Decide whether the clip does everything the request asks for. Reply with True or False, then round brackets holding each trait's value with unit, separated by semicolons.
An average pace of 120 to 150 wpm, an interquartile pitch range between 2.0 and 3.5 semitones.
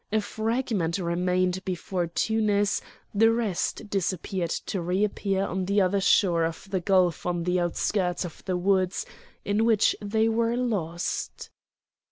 True (145 wpm; 2.9 semitones)